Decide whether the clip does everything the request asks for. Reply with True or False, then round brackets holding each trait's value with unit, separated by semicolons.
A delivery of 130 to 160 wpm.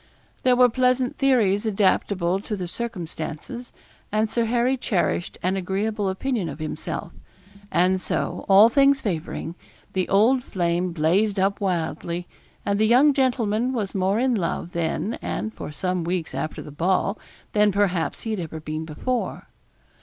True (155 wpm)